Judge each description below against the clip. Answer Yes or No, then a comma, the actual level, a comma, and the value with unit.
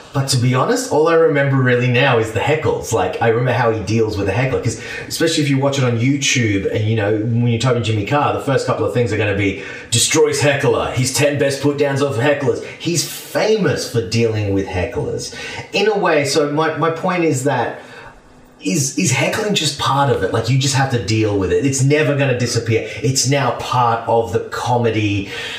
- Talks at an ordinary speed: No, fast, 230 wpm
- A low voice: Yes, low, 125 Hz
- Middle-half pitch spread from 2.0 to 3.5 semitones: No, average, 4.1 semitones